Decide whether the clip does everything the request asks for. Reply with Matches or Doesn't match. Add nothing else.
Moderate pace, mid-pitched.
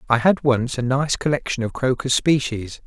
Doesn't match